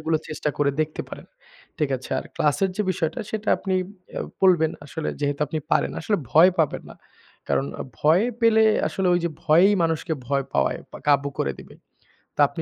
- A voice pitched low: No, medium, 160 Hz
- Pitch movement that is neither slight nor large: Yes, average, 4.2 semitones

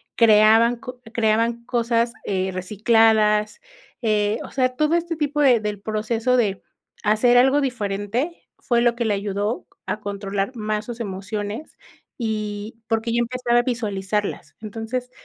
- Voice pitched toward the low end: No, high, 225 Hz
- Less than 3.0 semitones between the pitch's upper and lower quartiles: Yes, narrow, 2.5 semitones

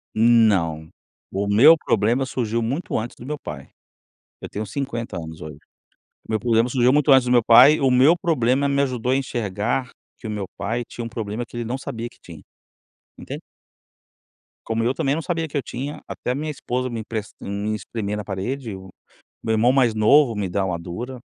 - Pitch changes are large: No, average, 4.0 semitones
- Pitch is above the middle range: No, low, 115 Hz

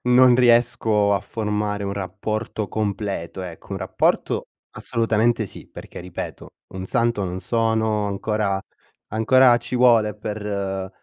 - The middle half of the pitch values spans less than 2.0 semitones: No, narrow, 2.5 semitones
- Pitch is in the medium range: No, low, 105 Hz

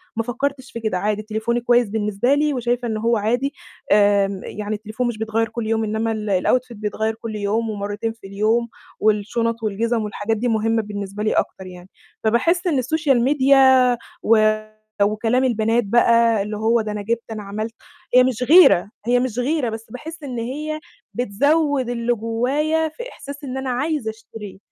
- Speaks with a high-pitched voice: Yes, high, 230 Hz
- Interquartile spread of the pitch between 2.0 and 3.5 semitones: Yes, average, 2.9 semitones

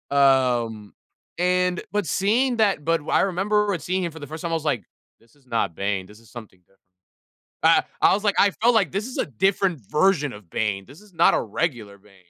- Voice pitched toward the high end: No, medium, 150 Hz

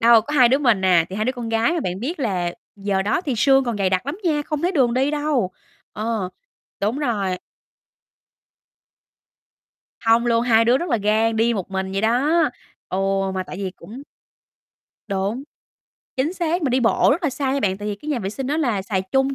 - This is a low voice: No, high, 235 Hz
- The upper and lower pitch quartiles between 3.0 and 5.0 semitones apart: No, wide, 5.5 semitones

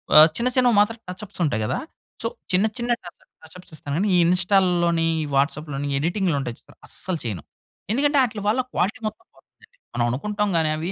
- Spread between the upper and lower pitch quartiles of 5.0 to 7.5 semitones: Yes, wide, 5.4 semitones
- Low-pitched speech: No, medium, 180 Hz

